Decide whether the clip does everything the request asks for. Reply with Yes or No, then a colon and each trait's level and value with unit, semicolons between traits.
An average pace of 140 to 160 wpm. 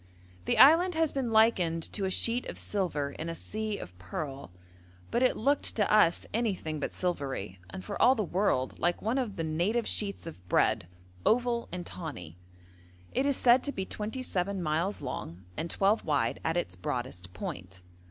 No: average, 180 wpm